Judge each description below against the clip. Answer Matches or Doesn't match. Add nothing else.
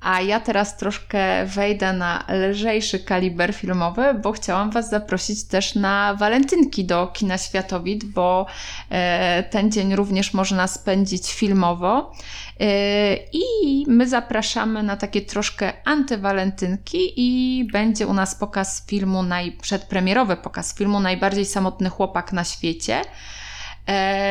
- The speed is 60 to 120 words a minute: Matches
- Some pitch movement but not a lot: Doesn't match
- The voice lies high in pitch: Matches